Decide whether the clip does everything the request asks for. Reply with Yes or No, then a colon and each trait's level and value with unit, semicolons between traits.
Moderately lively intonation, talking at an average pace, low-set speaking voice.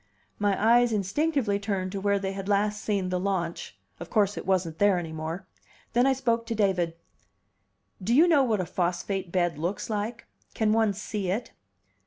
No: average, 3.2 semitones; average, 185 wpm; high, 200 Hz